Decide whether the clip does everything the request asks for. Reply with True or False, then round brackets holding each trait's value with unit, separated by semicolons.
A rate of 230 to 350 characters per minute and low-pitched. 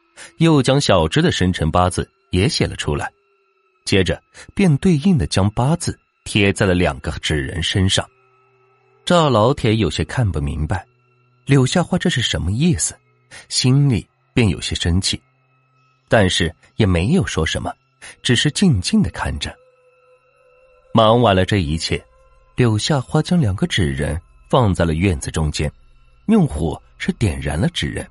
False (215 characters per minute; 125 Hz)